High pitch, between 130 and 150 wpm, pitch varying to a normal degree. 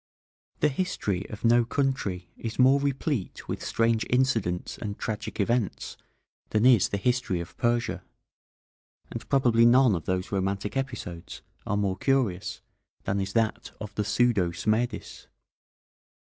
No: low, 110 Hz; slow, 135 wpm; average, 4.3 semitones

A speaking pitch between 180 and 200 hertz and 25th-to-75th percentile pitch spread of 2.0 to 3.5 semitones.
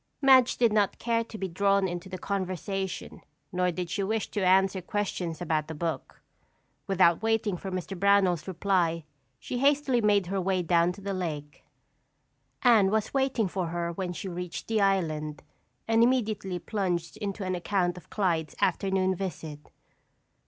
Yes: high, 190 Hz; average, 2.9 semitones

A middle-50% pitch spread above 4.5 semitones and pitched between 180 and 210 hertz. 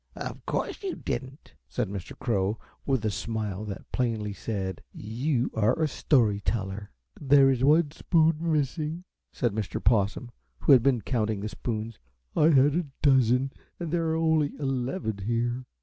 No: wide, 5.4 semitones; low, 125 Hz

